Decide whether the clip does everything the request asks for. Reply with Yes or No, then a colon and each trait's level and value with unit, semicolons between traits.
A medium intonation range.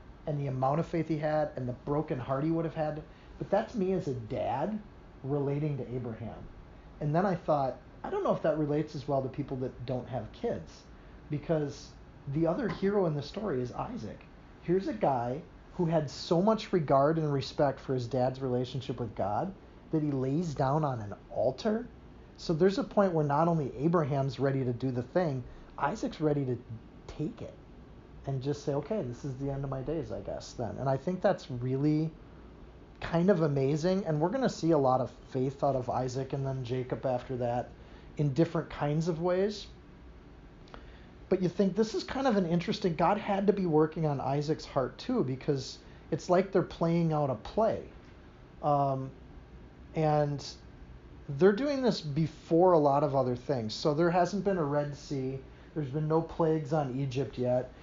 Yes: average, 4.3 semitones